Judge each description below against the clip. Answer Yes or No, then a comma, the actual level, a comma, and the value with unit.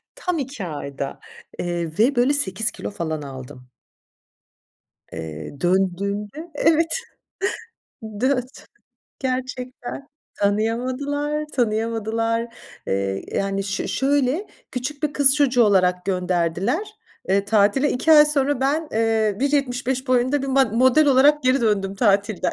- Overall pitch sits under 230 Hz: No, high, 235 Hz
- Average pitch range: No, wide, 5.9 semitones